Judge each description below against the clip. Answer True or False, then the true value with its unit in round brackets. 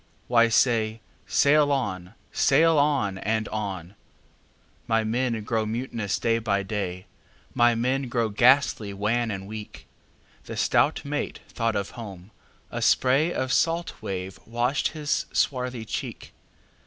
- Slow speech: True (115 wpm)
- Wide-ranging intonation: False (3.9 semitones)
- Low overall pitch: True (115 Hz)